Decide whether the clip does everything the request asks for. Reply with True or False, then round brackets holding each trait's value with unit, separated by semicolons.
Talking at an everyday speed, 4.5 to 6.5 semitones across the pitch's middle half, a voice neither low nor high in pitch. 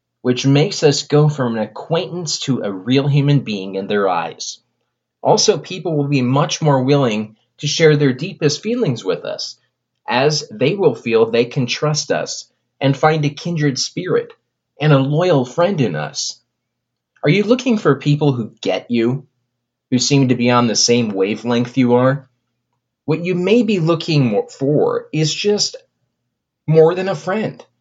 True (170 wpm; 5.4 semitones; 145 Hz)